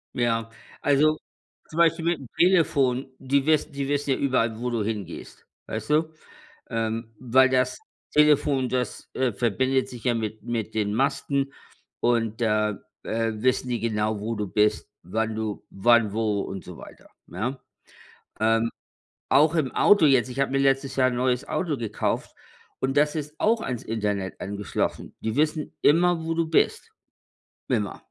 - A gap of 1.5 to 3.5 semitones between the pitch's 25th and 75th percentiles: No, average, 4.1 semitones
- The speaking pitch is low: Yes, low, 125 Hz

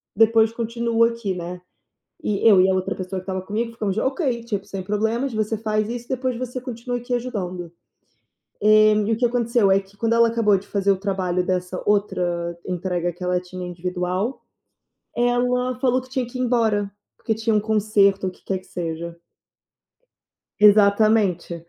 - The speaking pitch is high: Yes, high, 210 Hz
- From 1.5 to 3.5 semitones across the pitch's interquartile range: No, average, 3.9 semitones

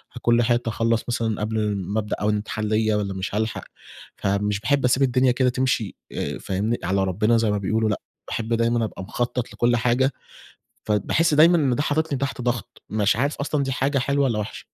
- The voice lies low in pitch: Yes, low, 115 Hz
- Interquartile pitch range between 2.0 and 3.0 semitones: No, average, 3.4 semitones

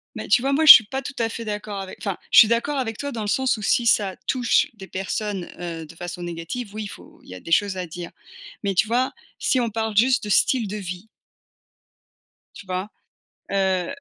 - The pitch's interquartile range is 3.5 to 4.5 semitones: Yes, average, 4.0 semitones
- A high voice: Yes, high, 210 Hz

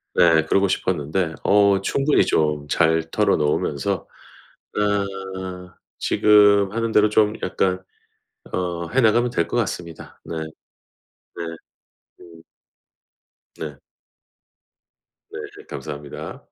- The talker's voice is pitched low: Yes, very low, 95 Hz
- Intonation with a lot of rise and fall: No, average, 4.5 semitones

